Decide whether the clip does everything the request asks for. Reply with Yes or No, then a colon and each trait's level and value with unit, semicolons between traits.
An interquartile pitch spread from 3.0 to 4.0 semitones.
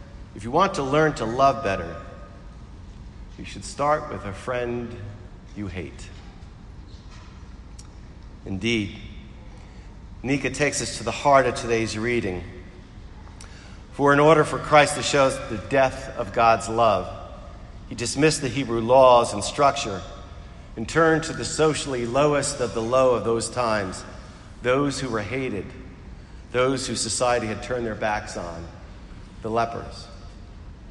No: average, 5.0 semitones